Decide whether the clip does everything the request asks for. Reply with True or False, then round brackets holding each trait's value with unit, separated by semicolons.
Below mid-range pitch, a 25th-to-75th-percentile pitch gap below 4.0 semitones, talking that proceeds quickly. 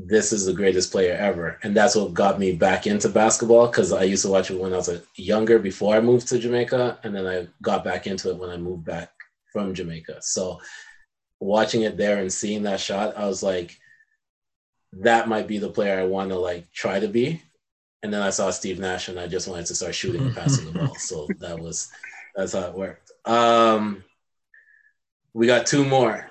False (105 Hz; 4.3 semitones; 215 wpm)